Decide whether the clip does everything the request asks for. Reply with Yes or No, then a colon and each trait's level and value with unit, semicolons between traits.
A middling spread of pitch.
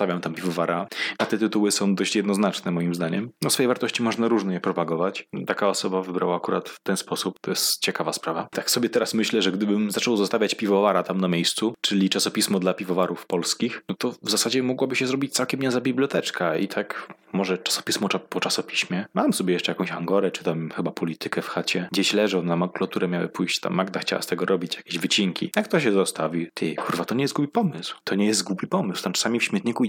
Yes: average, 3.8 semitones